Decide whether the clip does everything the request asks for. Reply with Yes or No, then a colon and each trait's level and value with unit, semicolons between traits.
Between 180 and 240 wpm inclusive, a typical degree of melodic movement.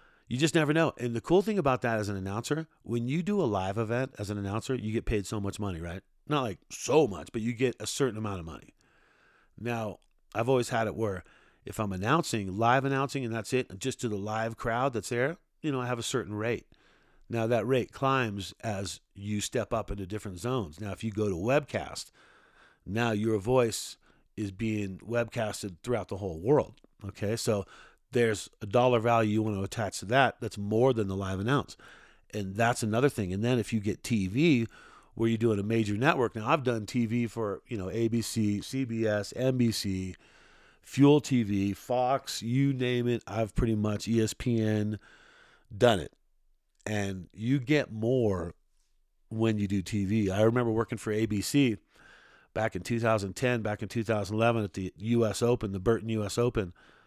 Yes: average, 190 wpm; average, 3.0 semitones